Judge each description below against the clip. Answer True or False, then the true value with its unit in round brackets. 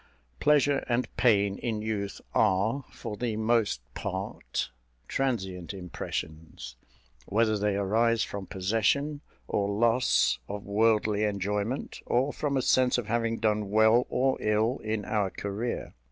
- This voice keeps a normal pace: False (130 wpm)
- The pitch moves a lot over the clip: False (2.8 semitones)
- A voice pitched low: True (110 Hz)